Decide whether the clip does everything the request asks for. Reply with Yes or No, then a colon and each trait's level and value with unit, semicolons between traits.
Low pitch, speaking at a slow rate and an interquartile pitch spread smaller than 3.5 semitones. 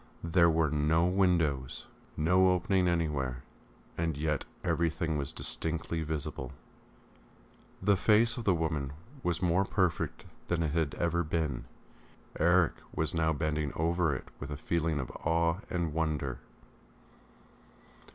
Yes: very low, 80 Hz; slow, 130 wpm; narrow, 2.5 semitones